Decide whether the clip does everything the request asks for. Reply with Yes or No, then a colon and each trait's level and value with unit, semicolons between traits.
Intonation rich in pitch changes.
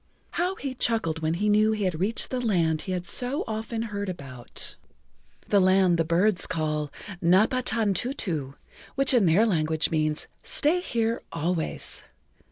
Yes: wide, 5.9 semitones